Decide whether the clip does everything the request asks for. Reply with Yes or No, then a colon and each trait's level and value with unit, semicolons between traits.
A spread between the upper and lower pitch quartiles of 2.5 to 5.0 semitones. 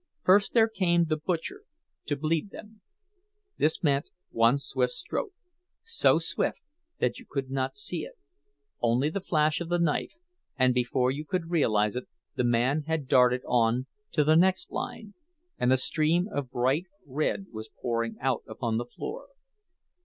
No: wide, 5.4 semitones